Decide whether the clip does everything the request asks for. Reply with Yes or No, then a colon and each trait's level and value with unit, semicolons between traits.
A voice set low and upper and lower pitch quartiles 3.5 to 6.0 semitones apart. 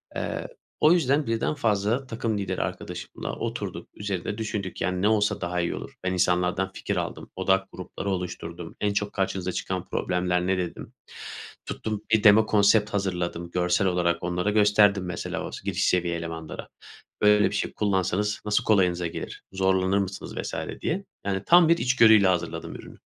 No: very low, 95 Hz; average, 2.7 semitones